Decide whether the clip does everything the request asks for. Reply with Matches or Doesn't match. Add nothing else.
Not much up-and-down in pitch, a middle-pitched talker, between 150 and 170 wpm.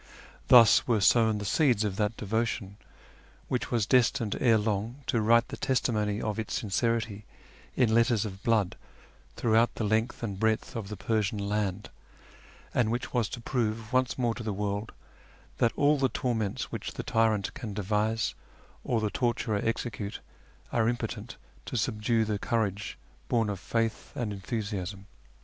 Doesn't match